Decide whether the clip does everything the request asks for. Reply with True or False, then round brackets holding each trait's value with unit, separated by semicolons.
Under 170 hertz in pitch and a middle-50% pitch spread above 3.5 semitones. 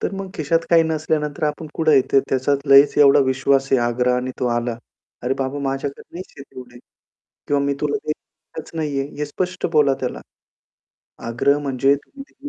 False (140 Hz; 2.8 semitones)